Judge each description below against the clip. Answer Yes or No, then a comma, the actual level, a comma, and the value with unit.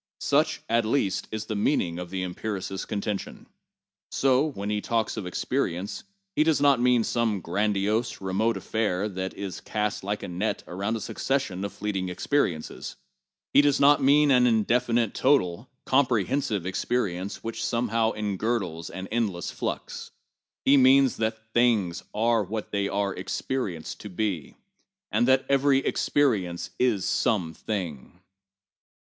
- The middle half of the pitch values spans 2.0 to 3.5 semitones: No, average, 4.5 semitones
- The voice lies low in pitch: Yes, low, 110 Hz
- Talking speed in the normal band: Yes, average, 145 wpm